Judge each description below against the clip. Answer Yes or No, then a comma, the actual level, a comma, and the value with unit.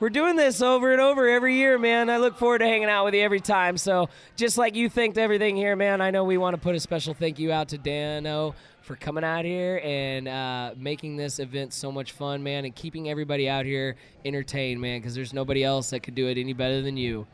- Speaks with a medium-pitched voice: Yes, medium, 155 Hz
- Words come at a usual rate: No, fast, 250 wpm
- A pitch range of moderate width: No, wide, 7.3 semitones